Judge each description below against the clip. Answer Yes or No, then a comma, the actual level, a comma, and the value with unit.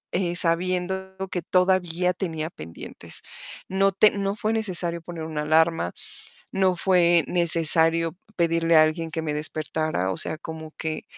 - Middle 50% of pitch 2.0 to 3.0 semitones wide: Yes, narrow, 2.4 semitones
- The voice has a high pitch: No, medium, 170 Hz